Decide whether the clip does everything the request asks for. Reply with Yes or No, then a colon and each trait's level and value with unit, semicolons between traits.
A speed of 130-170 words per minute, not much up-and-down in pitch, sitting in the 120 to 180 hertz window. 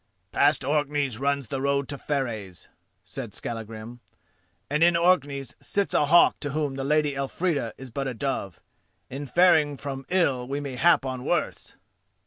Yes: average, 160 wpm; narrow, 2.3 semitones; medium, 140 Hz